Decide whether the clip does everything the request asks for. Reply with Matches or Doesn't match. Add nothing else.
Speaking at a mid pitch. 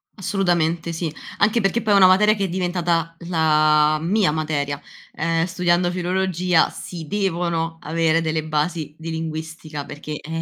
Matches